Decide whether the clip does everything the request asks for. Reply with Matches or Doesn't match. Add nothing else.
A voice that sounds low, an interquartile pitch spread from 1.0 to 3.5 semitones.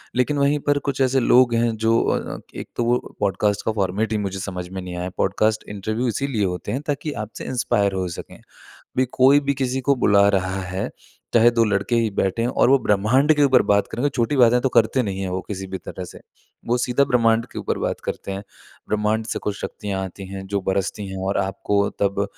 Doesn't match